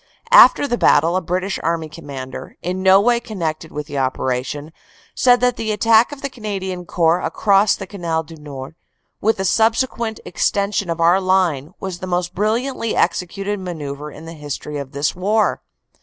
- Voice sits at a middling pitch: Yes, medium, 180 Hz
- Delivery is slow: No, average, 170 wpm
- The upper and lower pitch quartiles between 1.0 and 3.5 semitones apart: No, average, 5.1 semitones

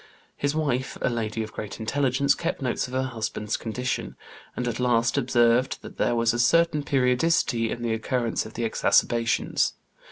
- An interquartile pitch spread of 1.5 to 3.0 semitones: Yes, narrow, 2.4 semitones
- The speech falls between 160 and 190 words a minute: Yes, average, 170 wpm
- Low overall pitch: Yes, low, 120 Hz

